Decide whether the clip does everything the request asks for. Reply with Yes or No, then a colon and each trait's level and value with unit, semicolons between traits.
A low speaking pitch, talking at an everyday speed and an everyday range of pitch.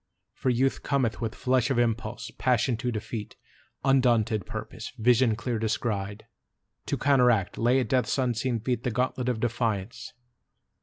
No: low, 120 Hz; average, 145 wpm; narrow, 2.3 semitones